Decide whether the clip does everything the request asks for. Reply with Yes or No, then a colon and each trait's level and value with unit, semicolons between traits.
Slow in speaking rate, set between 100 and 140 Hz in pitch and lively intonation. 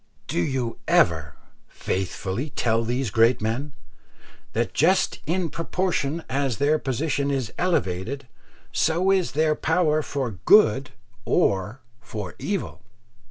Yes: slow, 115 wpm; low, 135 Hz; wide, 5.8 semitones